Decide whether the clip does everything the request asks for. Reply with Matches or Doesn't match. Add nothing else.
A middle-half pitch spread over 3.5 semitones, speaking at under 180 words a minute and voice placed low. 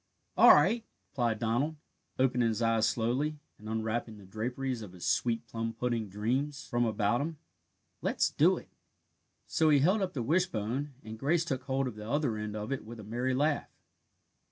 Doesn't match